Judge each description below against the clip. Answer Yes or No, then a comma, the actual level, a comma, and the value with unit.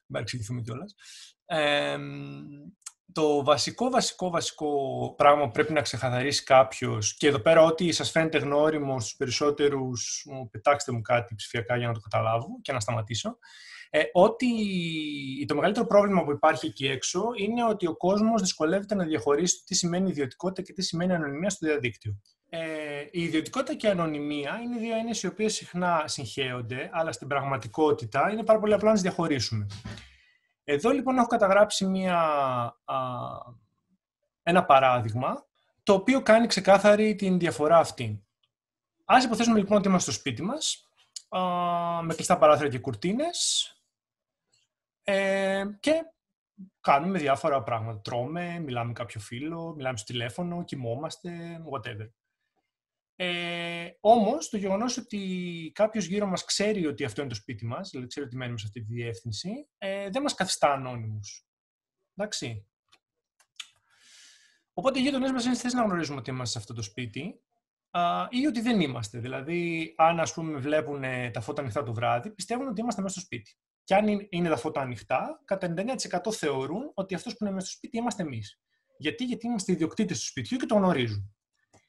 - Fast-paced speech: No, average, 150 wpm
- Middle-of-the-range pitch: Yes, medium, 160 Hz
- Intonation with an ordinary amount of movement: No, wide, 7.4 semitones